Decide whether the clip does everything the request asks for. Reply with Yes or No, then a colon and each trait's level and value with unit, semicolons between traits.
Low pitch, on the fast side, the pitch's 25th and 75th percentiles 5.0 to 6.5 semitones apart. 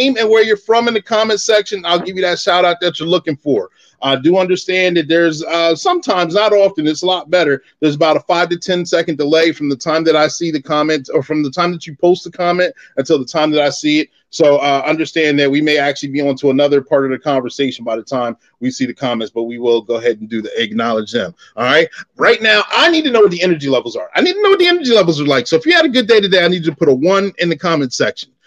No: medium, 165 Hz; fast, 290 wpm; wide, 5.4 semitones